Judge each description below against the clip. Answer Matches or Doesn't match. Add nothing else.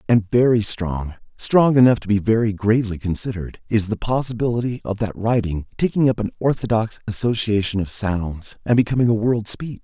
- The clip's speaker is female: Doesn't match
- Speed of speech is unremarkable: Matches